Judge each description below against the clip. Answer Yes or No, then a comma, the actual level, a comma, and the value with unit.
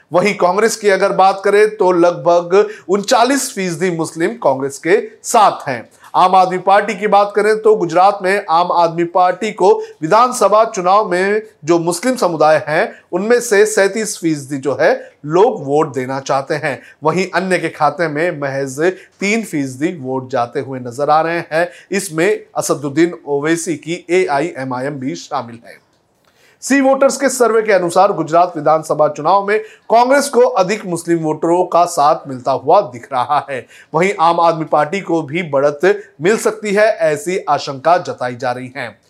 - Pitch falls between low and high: Yes, medium, 180 Hz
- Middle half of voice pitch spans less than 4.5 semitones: No, average, 4.8 semitones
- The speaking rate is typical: Yes, average, 165 wpm